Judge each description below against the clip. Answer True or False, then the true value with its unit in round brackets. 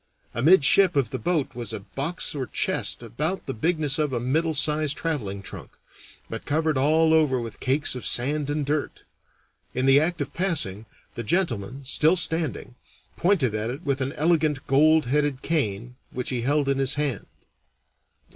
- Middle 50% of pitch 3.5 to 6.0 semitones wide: True (3.9 semitones)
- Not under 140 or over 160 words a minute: False (170 wpm)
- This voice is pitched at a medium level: True (145 Hz)